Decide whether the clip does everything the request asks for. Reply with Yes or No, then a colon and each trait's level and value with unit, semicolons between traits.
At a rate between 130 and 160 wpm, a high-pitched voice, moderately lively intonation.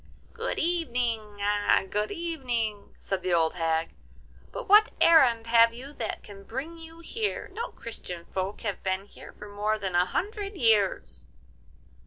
No: average, 150 wpm; high, 230 Hz; wide, 8.7 semitones